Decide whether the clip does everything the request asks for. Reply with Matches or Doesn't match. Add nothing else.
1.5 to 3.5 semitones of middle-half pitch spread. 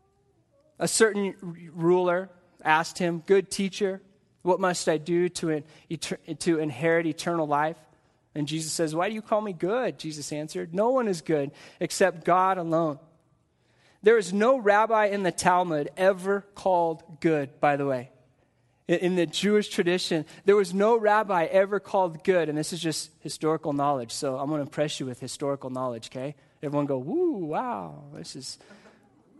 Doesn't match